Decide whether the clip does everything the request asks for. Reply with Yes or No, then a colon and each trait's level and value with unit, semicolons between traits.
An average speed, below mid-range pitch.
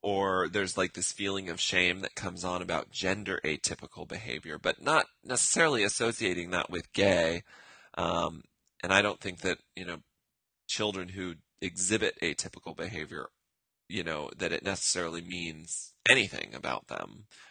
Yes: average, 145 wpm; very low, 90 Hz